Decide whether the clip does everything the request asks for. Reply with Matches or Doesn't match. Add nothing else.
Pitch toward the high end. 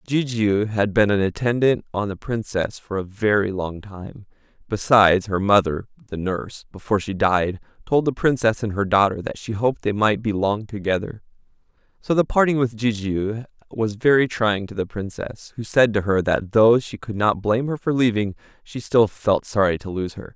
Doesn't match